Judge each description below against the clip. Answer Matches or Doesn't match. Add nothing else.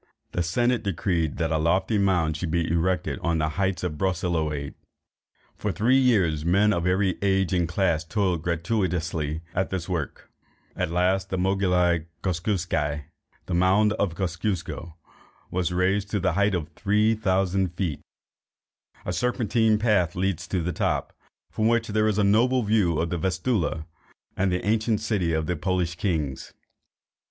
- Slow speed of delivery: Doesn't match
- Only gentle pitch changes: Doesn't match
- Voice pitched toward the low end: Matches